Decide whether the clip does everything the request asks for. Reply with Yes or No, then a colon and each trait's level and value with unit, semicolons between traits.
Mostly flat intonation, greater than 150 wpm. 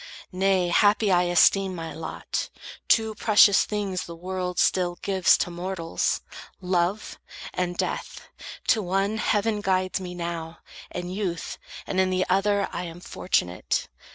No: narrow, 2.0 semitones; average, 140 wpm